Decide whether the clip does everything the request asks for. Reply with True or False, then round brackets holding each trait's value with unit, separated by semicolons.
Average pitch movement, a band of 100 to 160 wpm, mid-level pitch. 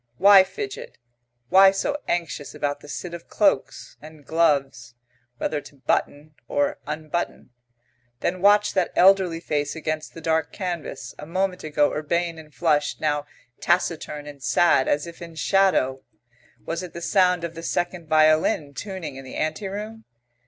True (3.7 semitones; 155 wpm; 165 Hz)